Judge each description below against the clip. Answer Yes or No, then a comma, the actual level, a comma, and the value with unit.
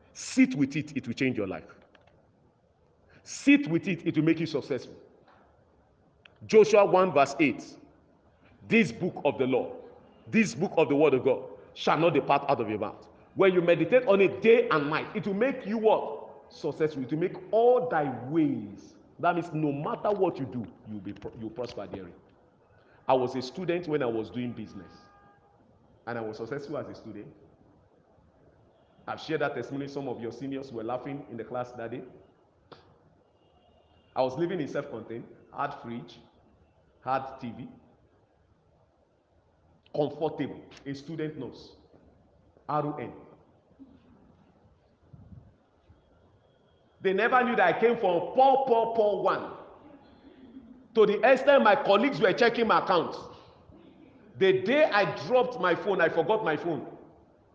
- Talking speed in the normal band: Yes, average, 155 wpm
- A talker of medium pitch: Yes, medium, 155 Hz